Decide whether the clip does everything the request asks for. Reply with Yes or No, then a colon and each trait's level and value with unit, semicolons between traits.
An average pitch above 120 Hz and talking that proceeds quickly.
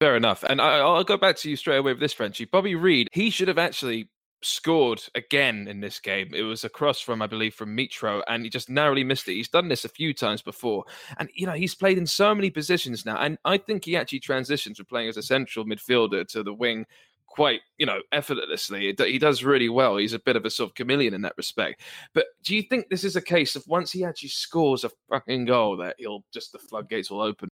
Yes: medium, 140 Hz; fast, 250 wpm